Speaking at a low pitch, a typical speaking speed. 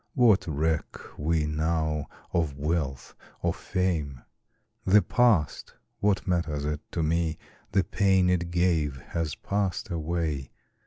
No: very low, 80 Hz; slow, 120 wpm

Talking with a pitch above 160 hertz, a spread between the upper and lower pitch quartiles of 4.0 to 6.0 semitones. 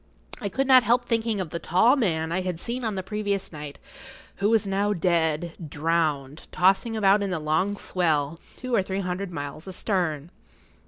Yes: medium, 185 Hz; average, 4.3 semitones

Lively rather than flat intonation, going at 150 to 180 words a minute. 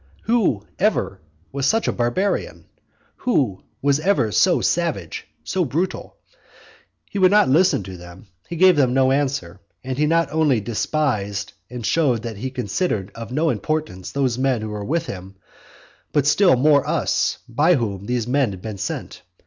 Yes: wide, 6.7 semitones; average, 165 wpm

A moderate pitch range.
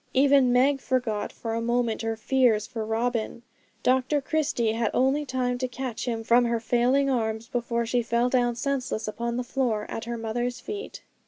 No: narrow, 2.1 semitones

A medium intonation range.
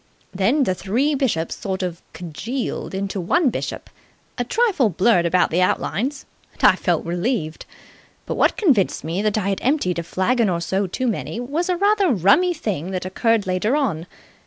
No: wide, 6.5 semitones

